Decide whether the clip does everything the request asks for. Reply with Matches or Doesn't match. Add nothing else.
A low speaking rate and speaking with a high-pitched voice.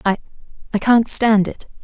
Matches